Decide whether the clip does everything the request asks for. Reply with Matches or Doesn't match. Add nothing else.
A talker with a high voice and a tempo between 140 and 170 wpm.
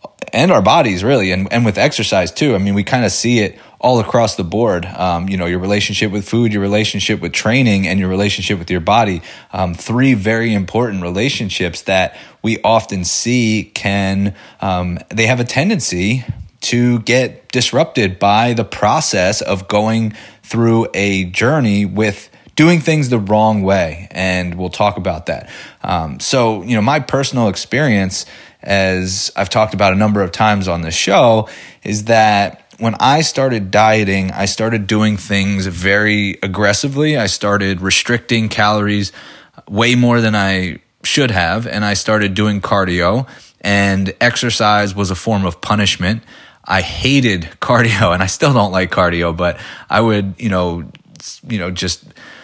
Doesn't match